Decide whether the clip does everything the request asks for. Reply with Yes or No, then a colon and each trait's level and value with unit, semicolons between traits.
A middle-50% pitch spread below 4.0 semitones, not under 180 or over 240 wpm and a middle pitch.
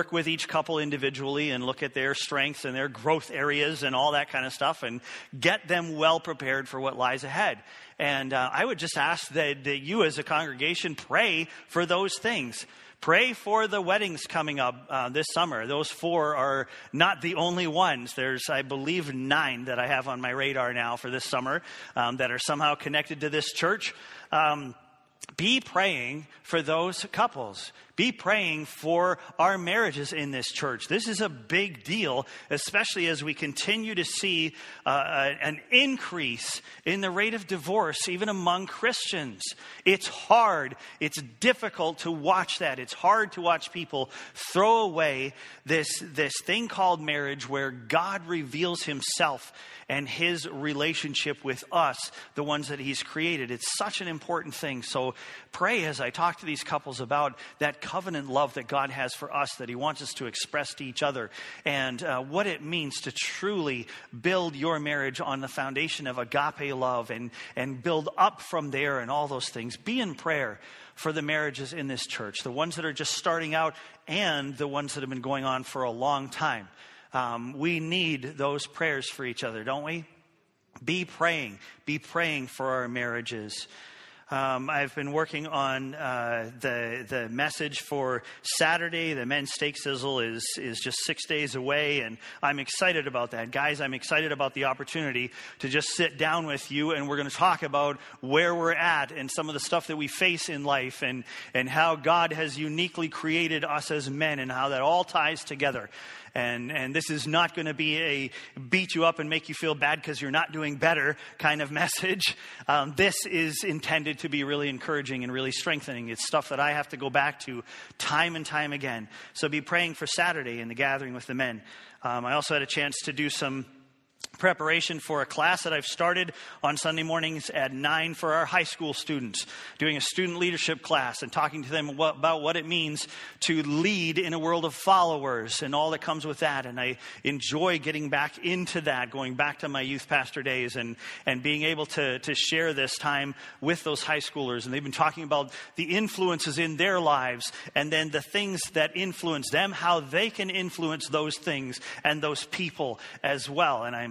Yes: average, 3.4 semitones; average, 195 wpm; medium, 150 Hz